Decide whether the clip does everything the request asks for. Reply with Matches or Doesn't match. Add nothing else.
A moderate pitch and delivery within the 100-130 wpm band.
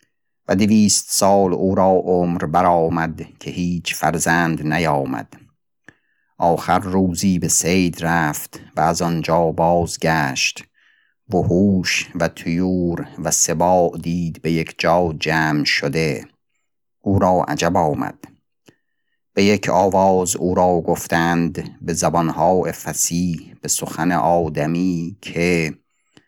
Doesn't match